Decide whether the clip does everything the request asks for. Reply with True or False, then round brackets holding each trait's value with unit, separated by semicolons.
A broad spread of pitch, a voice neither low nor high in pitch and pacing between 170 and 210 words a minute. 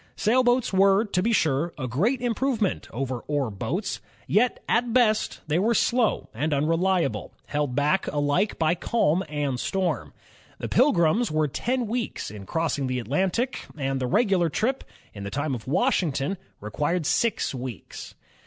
False (7.8 semitones; 170 Hz; 155 wpm)